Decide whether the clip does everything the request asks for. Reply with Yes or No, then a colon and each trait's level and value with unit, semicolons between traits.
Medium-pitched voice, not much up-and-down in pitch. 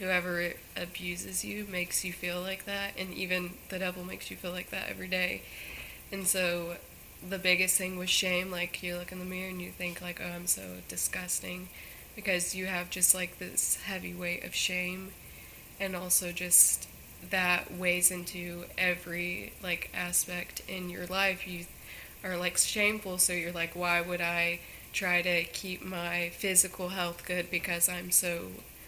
Yes: medium, 180 Hz; narrow, 0.8 semitones